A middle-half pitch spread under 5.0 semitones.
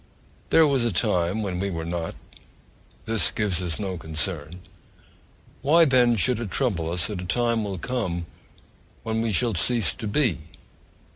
No: average, 5.3 semitones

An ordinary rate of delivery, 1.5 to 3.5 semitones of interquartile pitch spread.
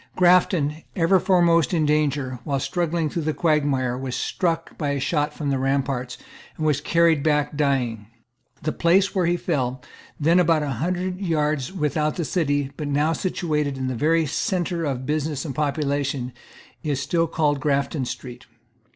Yes: average, 165 wpm; average, 3.2 semitones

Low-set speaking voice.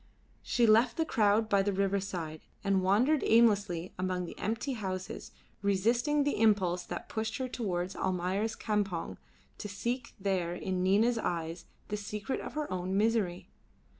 No: high, 200 Hz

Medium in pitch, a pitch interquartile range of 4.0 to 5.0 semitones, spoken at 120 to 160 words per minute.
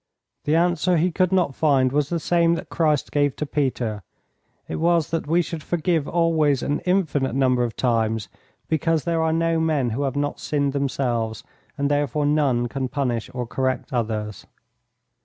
No: medium, 145 Hz; average, 4.3 semitones; average, 175 wpm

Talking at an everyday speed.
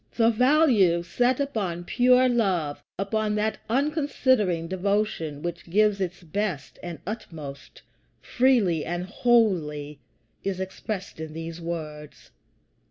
No: slow, 110 wpm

